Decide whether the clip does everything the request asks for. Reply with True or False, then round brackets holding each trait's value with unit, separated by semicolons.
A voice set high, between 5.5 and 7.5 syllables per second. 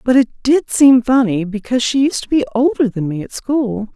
False (250 Hz; 5.3 syllables/s)